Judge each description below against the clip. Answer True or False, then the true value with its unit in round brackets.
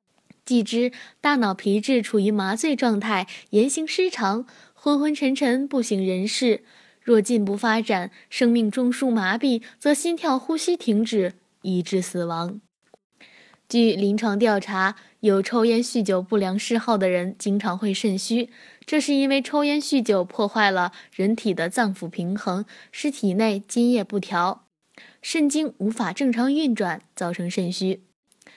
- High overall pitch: True (220 Hz)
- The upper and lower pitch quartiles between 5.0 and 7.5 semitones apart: False (4.5 semitones)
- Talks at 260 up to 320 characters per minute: False (220 characters per minute)